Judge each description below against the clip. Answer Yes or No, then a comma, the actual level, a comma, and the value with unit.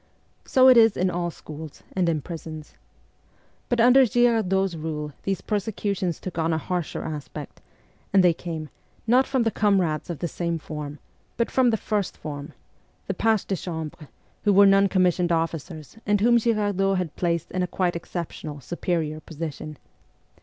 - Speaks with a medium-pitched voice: Yes, medium, 180 Hz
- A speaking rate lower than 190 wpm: Yes, average, 165 wpm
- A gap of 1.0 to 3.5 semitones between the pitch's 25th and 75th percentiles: No, average, 4.2 semitones